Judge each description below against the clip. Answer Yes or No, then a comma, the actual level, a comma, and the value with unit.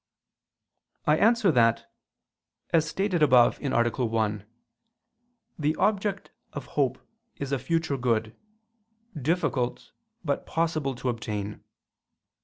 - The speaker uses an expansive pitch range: Yes, wide, 5.7 semitones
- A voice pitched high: No, medium, 140 Hz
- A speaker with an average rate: No, slow, 100 wpm